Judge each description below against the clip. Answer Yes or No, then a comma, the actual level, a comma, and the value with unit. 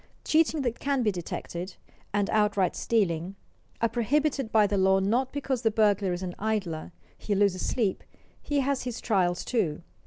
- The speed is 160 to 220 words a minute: Yes, average, 165 wpm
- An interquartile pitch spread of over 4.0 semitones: Yes, average, 4.6 semitones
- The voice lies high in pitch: Yes, high, 210 Hz